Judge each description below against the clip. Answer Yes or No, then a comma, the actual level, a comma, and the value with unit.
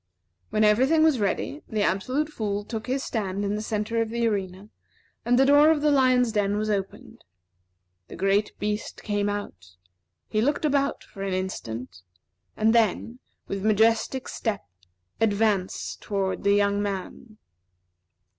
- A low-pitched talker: No, high, 215 Hz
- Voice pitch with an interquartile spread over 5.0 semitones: No, average, 3.4 semitones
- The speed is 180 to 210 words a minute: No, average, 155 wpm